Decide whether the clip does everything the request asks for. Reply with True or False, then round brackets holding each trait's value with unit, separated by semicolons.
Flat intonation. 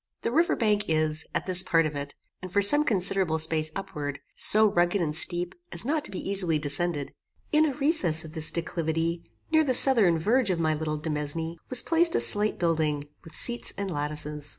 False (5.0 semitones)